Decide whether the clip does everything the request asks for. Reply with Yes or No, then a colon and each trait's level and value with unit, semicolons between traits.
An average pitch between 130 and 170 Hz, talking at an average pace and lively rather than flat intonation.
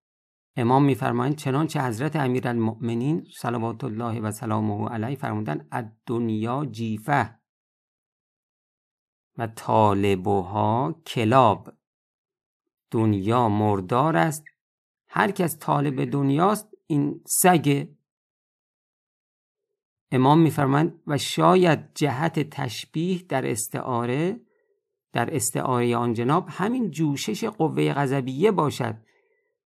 No: low, 135 Hz; slow, 90 wpm; wide, 5.7 semitones